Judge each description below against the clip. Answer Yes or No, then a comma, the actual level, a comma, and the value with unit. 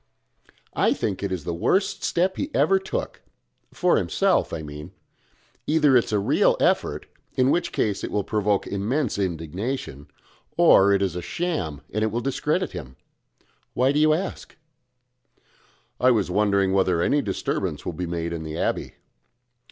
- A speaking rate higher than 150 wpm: Yes, average, 160 wpm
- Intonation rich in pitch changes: Yes, wide, 7.6 semitones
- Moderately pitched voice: No, low, 100 Hz